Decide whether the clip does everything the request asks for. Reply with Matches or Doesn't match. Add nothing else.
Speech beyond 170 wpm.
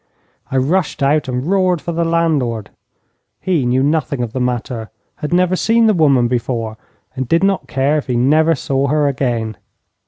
Matches